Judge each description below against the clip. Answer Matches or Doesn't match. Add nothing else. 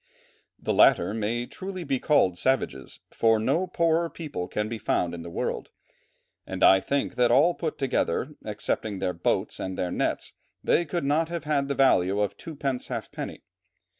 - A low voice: Matches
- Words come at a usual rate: Matches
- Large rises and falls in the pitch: Matches